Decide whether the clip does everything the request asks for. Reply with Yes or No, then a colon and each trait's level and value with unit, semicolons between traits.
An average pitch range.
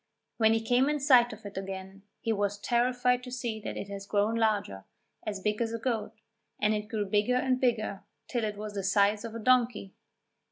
Yes: average, 3.1 semitones